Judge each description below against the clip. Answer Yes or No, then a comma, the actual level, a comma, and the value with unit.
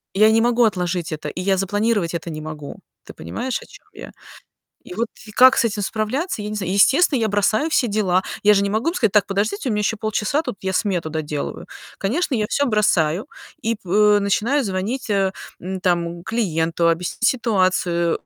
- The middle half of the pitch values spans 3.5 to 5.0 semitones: Yes, average, 4.0 semitones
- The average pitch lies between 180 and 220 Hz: Yes, high, 205 Hz